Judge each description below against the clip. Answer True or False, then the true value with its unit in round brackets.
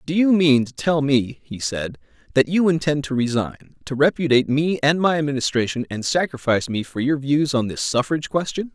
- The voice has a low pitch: False (145 Hz)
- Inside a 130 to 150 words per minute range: False (200 wpm)